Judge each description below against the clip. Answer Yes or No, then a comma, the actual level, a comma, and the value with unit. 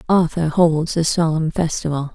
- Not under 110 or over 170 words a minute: Yes, average, 140 wpm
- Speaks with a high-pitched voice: No, medium, 160 Hz